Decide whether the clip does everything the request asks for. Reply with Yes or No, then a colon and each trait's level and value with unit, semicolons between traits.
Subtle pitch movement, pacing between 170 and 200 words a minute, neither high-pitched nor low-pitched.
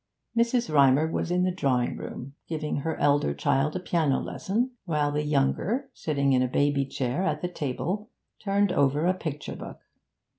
No: average, 4.7 semitones; average, 175 wpm; medium, 150 Hz